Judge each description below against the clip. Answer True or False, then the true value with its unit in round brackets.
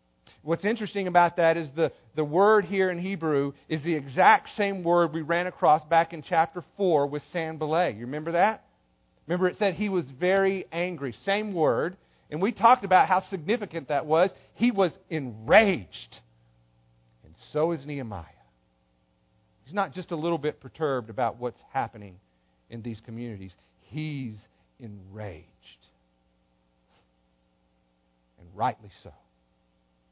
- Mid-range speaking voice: True (145 Hz)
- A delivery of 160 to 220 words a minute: False (140 wpm)